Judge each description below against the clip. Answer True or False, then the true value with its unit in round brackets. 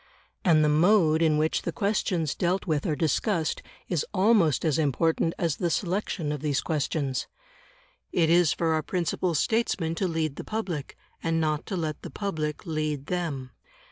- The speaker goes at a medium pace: True (170 wpm)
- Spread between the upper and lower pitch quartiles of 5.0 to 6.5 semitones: False (2.7 semitones)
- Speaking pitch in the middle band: True (160 Hz)